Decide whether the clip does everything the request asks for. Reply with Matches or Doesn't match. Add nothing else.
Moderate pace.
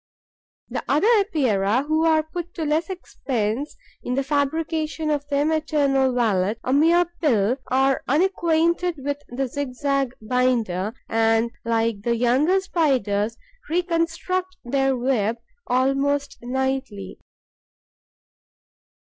Doesn't match